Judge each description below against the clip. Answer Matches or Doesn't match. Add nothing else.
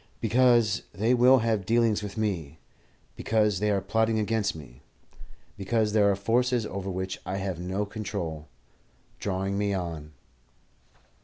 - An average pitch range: Matches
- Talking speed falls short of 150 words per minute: Matches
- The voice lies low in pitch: Matches